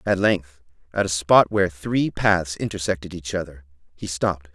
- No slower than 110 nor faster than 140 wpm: No, average, 170 wpm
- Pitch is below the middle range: Yes, very low, 90 Hz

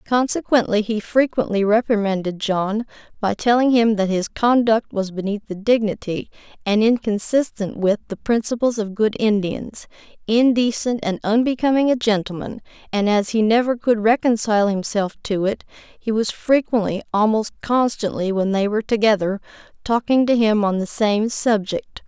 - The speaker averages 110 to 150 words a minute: Yes, average, 145 wpm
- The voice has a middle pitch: No, high, 215 Hz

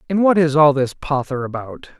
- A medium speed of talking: No, fast, 210 wpm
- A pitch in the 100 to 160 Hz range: Yes, medium, 145 Hz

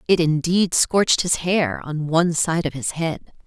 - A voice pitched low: No, medium, 165 Hz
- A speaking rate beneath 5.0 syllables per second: Yes, 4.4 syllables/s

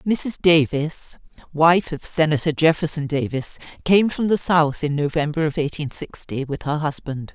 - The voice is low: No, medium, 155 Hz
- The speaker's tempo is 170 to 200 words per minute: No, average, 155 wpm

